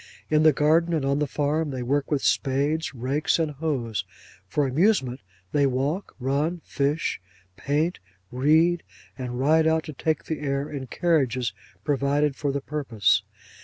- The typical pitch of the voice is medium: Yes, medium, 145 Hz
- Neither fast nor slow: Yes, average, 155 wpm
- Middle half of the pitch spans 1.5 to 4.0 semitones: Yes, average, 2.9 semitones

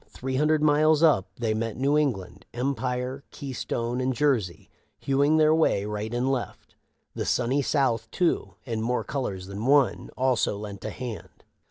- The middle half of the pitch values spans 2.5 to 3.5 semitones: No, average, 4.1 semitones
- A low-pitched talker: Yes, low, 125 Hz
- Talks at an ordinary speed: Yes, average, 160 wpm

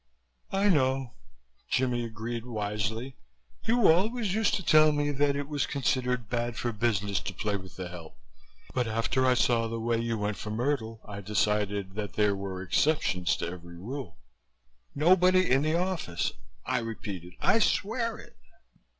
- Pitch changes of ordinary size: No, wide, 5.9 semitones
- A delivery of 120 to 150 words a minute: No, average, 160 wpm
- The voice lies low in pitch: Yes, low, 120 Hz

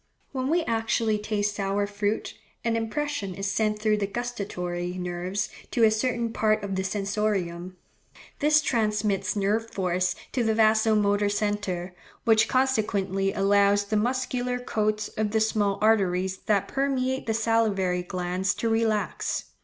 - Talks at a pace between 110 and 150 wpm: Yes, average, 140 wpm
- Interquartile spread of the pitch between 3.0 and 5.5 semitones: No, narrow, 2.5 semitones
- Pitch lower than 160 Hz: No, high, 210 Hz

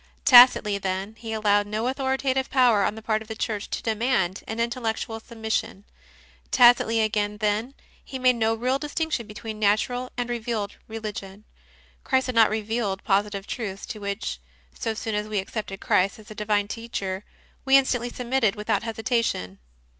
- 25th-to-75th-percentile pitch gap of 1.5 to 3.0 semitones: Yes, average, 2.7 semitones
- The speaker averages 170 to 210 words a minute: No, average, 160 wpm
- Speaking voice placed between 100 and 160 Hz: No, high, 220 Hz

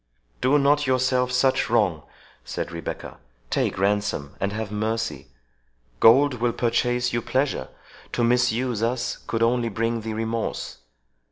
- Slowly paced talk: Yes, slow, 125 wpm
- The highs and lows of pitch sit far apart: No, average, 2.9 semitones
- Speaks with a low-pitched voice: Yes, low, 115 Hz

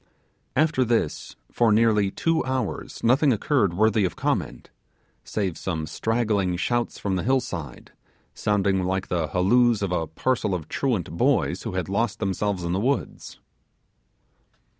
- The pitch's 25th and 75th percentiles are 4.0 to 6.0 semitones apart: Yes, average, 4.7 semitones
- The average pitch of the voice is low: Yes, low, 105 Hz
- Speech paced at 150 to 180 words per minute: No, average, 140 wpm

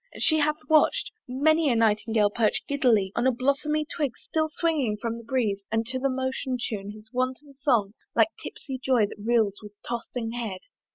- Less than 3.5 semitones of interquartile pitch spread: No, average, 4.3 semitones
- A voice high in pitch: Yes, high, 245 Hz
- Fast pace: No, average, 180 wpm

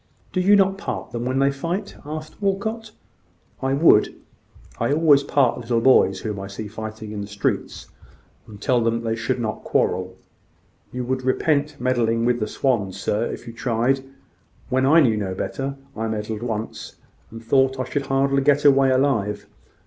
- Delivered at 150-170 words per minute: No, average, 180 wpm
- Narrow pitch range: No, average, 4.0 semitones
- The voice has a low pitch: Yes, low, 125 Hz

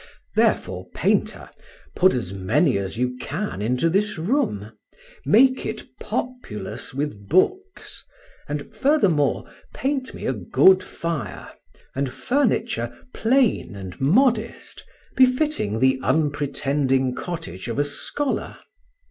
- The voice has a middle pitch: Yes, medium, 150 Hz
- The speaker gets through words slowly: Yes, slow, 110 wpm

